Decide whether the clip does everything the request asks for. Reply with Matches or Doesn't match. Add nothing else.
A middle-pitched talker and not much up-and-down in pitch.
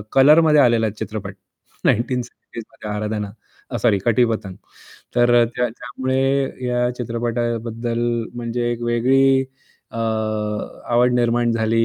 Doesn't match